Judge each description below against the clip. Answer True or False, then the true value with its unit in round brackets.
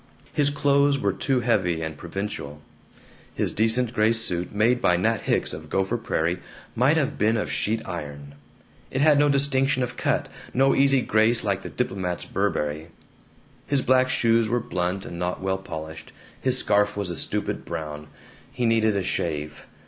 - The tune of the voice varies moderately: False (6.3 semitones)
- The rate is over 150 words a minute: True (170 wpm)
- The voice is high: False (105 Hz)